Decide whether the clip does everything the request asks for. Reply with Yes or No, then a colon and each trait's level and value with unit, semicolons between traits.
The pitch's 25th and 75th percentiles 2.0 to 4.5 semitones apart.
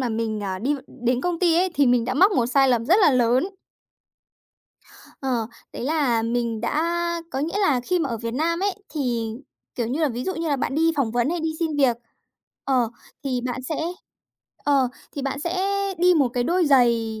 No: average, 5.3 semitones